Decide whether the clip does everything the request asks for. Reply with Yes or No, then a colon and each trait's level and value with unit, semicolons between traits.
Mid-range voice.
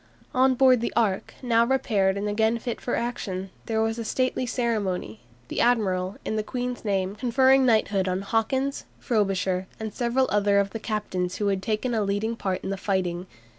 No: high, 215 Hz